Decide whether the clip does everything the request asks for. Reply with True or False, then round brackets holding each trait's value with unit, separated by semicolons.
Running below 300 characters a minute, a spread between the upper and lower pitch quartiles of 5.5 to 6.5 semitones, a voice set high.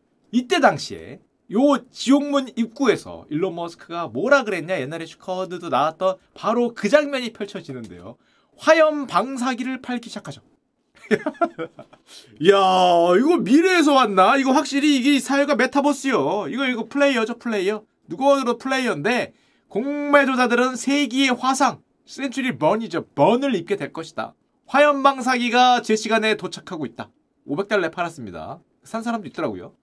False (330 characters per minute; 6.2 semitones; 245 Hz)